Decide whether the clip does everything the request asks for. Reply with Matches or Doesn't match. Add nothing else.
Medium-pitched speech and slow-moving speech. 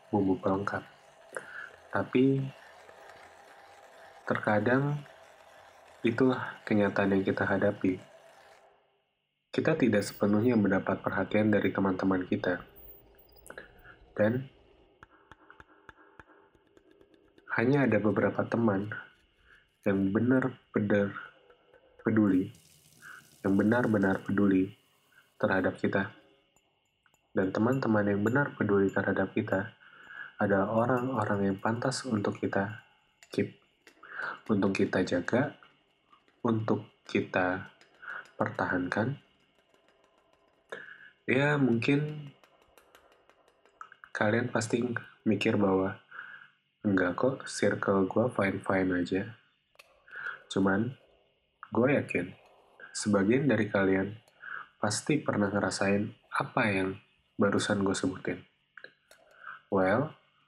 Doesn't match